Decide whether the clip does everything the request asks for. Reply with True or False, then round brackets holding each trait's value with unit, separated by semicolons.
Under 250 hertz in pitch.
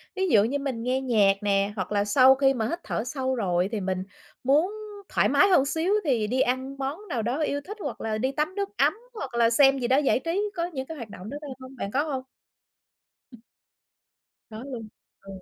False (260 Hz)